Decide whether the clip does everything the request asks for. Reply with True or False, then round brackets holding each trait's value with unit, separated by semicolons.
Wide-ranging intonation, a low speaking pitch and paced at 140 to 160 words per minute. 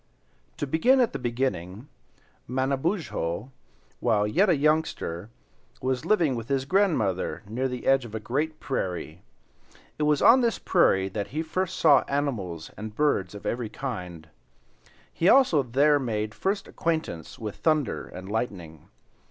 True (6.8 semitones; 130 Hz; 145 wpm)